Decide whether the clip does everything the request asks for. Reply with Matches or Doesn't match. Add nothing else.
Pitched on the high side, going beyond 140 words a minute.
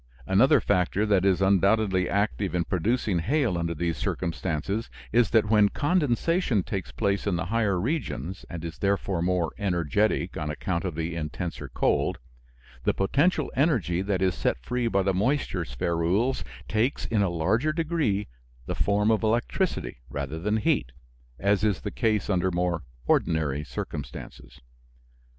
Doesn't match